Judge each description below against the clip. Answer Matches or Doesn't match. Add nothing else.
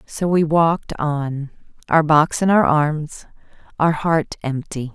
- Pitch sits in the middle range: Matches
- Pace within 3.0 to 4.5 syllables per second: Matches